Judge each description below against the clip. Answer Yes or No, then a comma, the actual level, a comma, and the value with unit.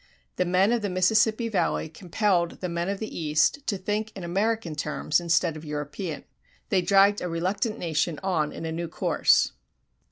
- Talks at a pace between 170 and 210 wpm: Yes, average, 180 wpm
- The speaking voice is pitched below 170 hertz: No, medium, 180 Hz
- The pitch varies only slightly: No, average, 3.7 semitones